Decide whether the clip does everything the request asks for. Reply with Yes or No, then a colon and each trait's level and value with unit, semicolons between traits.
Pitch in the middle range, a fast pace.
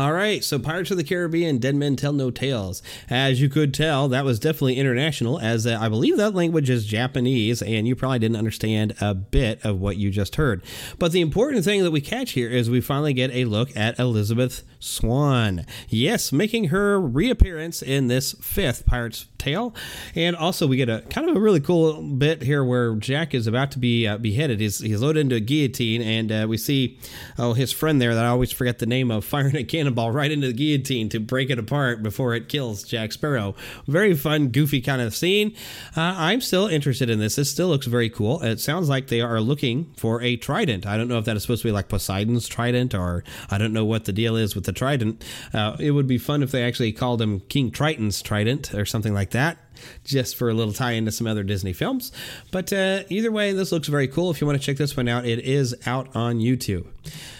No: low, 125 Hz; fast, 230 wpm